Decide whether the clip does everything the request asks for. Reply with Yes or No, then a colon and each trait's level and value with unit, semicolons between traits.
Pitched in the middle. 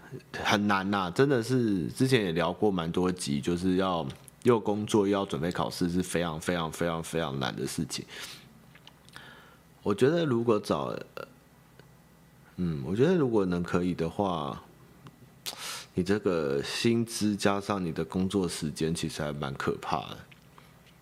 No: very low, 95 Hz